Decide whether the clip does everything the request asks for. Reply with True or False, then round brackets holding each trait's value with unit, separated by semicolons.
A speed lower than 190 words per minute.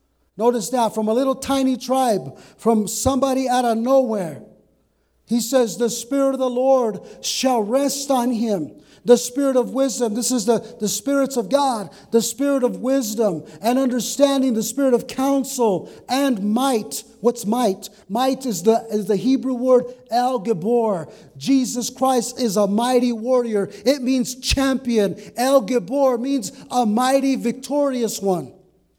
True (150 wpm)